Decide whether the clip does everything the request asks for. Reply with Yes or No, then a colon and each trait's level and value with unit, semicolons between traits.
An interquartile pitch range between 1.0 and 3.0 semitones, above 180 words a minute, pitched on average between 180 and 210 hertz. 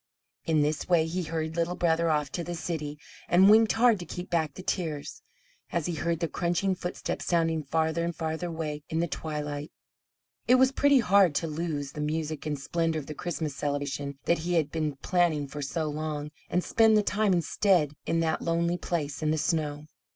No: narrow, 2.6 semitones; average, 200 wpm; medium, 165 Hz